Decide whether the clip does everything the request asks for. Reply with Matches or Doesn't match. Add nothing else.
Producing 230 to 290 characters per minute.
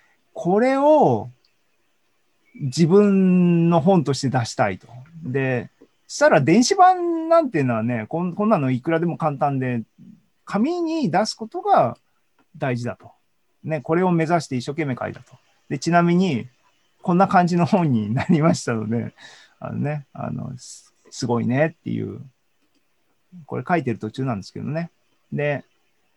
Matches